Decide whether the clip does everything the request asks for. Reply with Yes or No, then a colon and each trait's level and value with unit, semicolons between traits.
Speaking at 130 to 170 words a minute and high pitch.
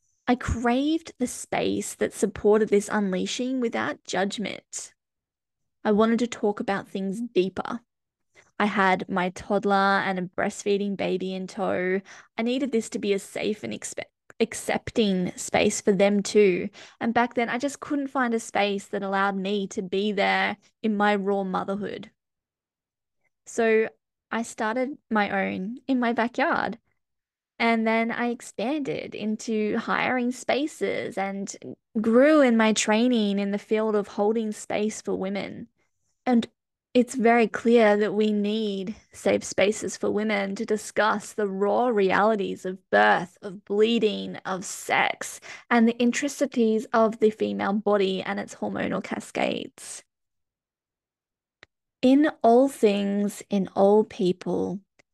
Yes: average, 140 wpm; high, 215 Hz